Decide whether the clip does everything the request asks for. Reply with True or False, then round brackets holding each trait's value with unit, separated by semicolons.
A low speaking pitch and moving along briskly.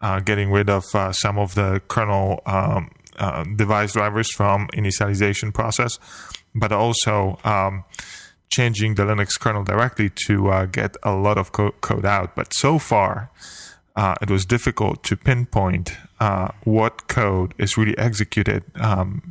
False (105 Hz; 150 wpm)